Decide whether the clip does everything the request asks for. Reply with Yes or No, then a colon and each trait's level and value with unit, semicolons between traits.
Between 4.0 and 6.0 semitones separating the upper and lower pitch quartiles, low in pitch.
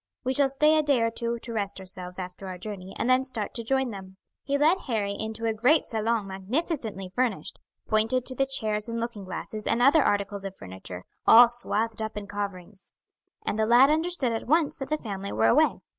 No: average, 4.5 semitones; high, 225 Hz